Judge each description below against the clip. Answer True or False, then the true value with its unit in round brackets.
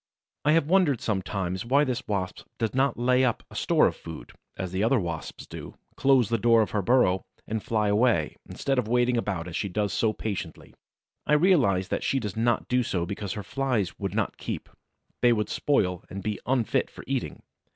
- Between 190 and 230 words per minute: True (205 wpm)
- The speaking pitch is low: True (110 Hz)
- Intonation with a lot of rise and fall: False (4.5 semitones)